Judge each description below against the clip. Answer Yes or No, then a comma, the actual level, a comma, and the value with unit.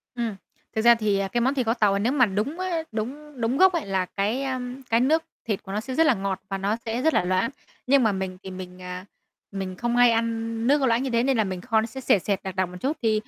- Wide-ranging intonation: No, average, 4.7 semitones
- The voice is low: No, high, 225 Hz